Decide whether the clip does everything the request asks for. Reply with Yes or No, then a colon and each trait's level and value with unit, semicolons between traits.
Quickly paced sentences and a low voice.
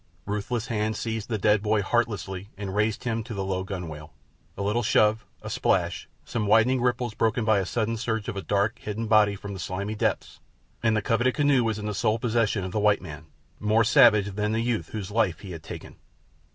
Yes: fast, 210 wpm; low, 105 Hz